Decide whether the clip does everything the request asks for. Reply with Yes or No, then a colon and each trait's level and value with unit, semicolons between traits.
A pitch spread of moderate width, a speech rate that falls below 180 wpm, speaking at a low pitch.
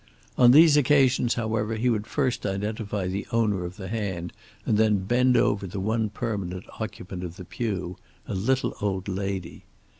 Yes: average, 3.6 semitones; average, 170 wpm; low, 105 Hz